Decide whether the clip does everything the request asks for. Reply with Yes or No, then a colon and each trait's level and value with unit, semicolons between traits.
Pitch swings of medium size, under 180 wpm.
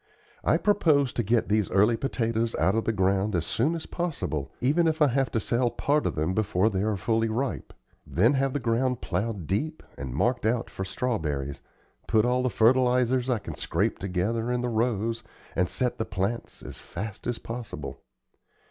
No: average, 4.5 semitones; average, 190 wpm